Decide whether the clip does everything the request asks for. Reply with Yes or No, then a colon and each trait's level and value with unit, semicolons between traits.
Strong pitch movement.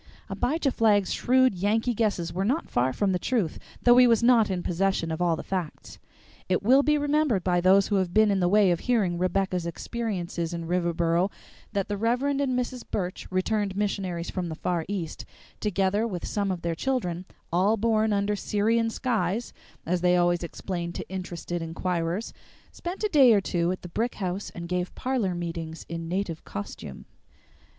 No: average, 4.3 semitones